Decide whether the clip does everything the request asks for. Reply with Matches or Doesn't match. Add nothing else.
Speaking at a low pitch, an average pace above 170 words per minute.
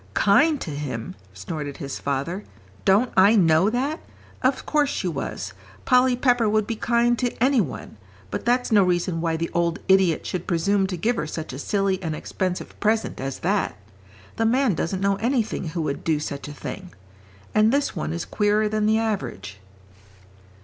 Doesn't match